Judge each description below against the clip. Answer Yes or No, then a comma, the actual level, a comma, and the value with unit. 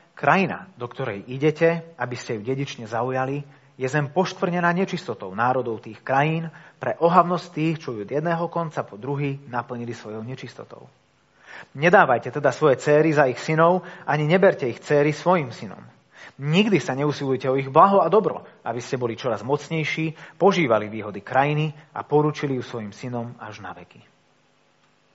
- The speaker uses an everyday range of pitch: Yes, average, 4.8 semitones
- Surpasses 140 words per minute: Yes, average, 160 wpm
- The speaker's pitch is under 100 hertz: No, medium, 140 Hz